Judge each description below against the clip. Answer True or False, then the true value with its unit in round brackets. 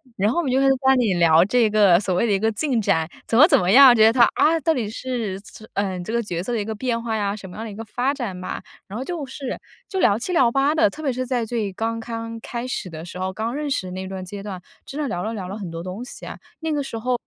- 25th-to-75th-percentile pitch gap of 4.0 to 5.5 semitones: True (4.8 semitones)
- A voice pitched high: True (225 Hz)